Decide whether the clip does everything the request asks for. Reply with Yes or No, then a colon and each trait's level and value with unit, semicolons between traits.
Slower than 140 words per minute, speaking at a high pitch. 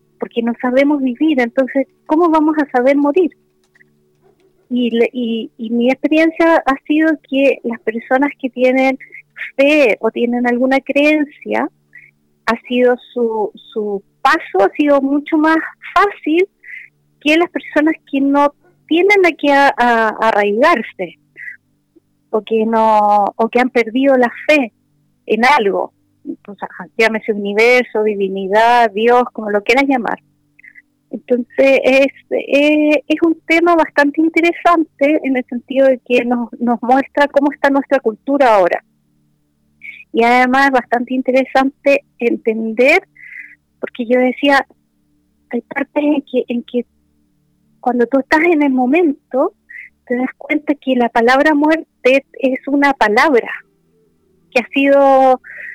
Yes: average, 130 wpm; very high, 260 Hz